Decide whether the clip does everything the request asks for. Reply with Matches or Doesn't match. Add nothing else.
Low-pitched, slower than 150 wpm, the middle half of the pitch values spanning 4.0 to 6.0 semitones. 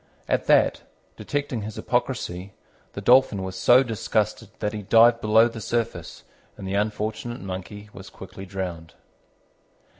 Doesn't match